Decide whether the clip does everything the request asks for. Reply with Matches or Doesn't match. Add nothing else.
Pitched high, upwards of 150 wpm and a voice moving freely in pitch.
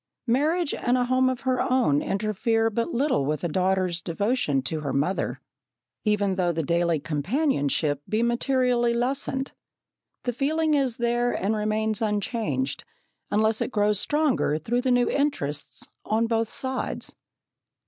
Doesn't match